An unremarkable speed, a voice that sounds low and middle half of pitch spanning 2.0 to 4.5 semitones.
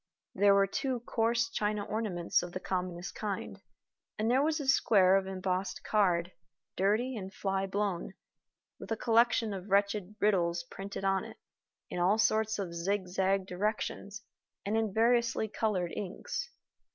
No: average, 150 wpm; high, 200 Hz; average, 2.7 semitones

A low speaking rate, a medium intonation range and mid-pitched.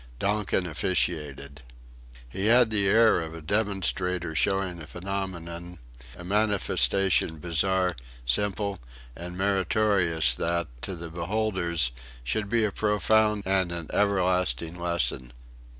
No: slow, 115 wpm; average, 3.1 semitones; very low, 90 Hz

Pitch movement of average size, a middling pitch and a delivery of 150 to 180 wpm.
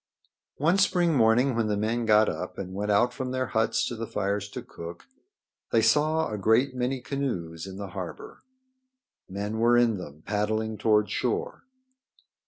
No: average, 3.8 semitones; low, 110 Hz; average, 170 wpm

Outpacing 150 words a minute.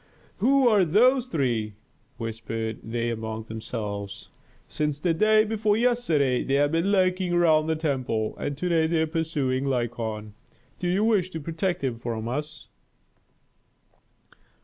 No: average, 145 wpm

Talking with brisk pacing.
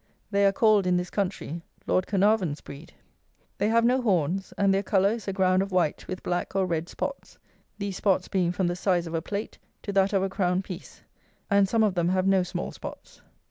Yes: fast, 220 wpm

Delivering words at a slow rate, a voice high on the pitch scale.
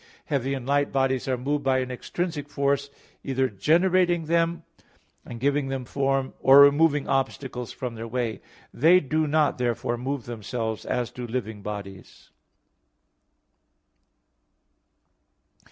No: slow, 125 wpm; low, 135 Hz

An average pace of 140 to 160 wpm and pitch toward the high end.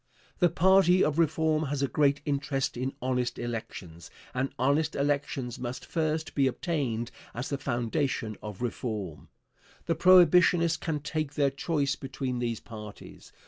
No: average, 145 wpm; medium, 140 Hz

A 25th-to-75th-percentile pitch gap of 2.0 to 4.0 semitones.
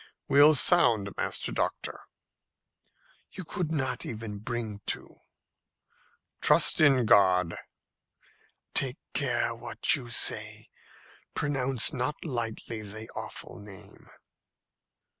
No: average, 4.6 semitones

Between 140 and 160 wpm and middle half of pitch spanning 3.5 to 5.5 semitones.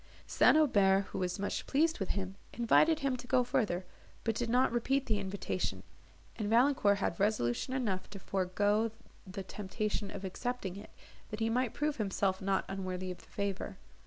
No: average, 175 wpm; average, 4.2 semitones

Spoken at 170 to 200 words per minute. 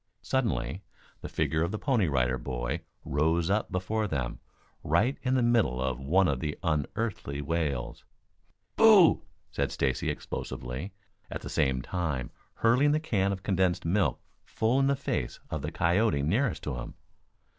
No: average, 155 wpm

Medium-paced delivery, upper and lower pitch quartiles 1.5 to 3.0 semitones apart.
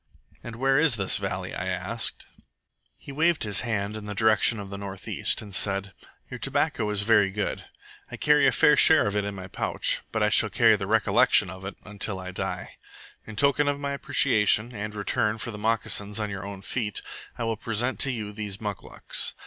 No: fast, 210 wpm; average, 2.7 semitones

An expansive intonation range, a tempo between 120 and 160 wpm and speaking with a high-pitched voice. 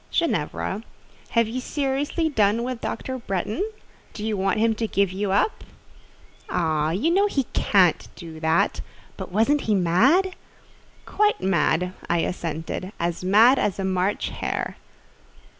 Yes: wide, 6.1 semitones; average, 140 wpm; high, 205 Hz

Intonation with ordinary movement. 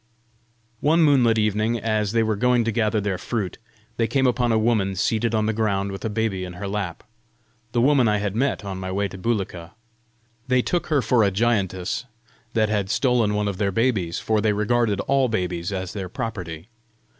Yes: average, 3.3 semitones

